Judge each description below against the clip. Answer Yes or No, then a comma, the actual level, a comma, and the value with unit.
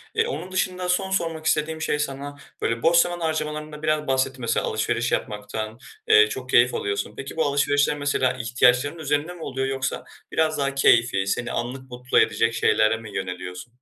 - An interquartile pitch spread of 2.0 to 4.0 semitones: No, average, 4.8 semitones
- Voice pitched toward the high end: No, medium, 145 Hz